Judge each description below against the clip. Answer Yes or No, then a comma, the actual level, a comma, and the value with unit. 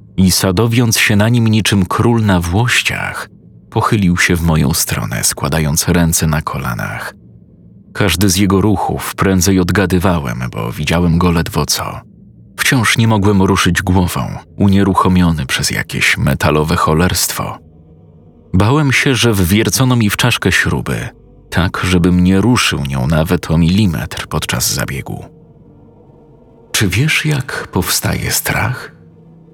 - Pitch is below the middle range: Yes, very low, 95 Hz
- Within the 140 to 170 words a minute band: No, average, 125 wpm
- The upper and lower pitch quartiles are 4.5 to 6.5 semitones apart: Yes, average, 5.0 semitones